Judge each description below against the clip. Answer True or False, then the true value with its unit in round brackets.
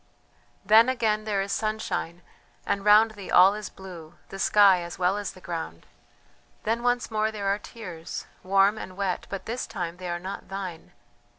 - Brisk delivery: False (180 wpm)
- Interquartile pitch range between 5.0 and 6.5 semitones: False (3.0 semitones)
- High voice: True (195 Hz)